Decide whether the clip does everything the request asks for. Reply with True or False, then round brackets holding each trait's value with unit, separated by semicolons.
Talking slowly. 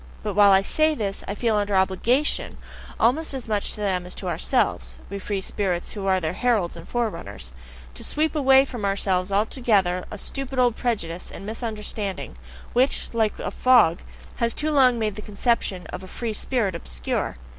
False (175 wpm)